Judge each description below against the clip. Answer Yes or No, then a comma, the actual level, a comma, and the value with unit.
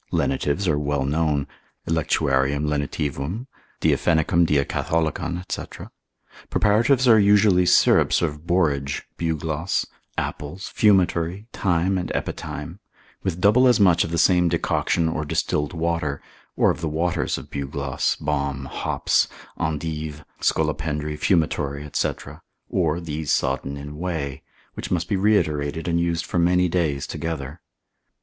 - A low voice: Yes, very low, 80 Hz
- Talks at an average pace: No, slow, 125 wpm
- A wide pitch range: No, average, 3.3 semitones